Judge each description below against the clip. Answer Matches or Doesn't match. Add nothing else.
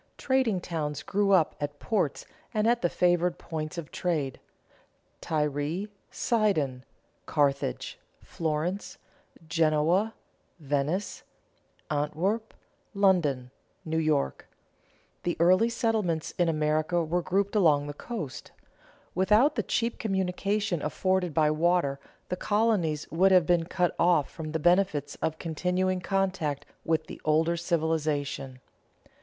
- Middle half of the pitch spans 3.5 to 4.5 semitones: Matches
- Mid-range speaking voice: Matches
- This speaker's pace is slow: Matches